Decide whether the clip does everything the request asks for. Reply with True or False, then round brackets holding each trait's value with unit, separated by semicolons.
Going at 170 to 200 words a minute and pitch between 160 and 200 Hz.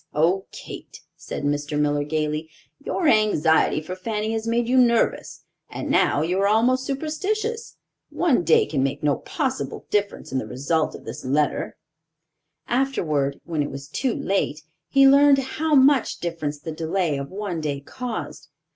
False (160 wpm; 185 Hz)